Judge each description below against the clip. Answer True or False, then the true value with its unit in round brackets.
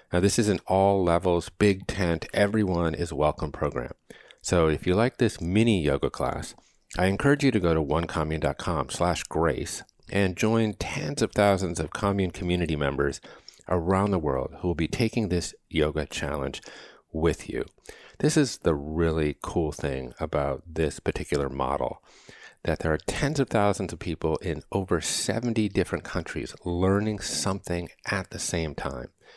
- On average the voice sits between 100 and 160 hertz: False (90 Hz)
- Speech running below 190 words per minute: True (155 wpm)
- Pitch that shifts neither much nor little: True (4.3 semitones)